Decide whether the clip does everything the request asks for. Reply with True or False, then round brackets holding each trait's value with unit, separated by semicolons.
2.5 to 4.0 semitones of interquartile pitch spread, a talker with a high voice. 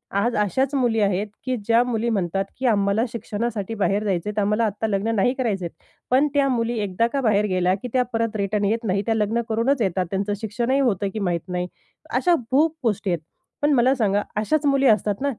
True (3.5 semitones; 220 Hz)